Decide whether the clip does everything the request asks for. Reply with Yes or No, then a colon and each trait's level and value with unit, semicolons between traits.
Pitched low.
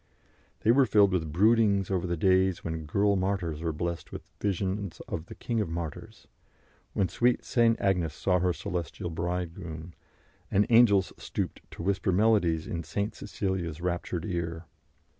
Yes: very low, 90 Hz